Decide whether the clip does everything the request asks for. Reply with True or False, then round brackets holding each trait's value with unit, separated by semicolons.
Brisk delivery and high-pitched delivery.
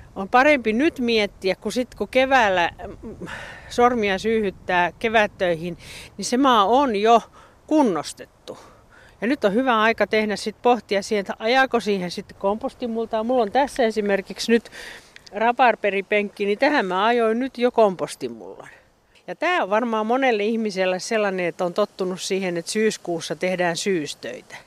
False (145 wpm; 220 Hz)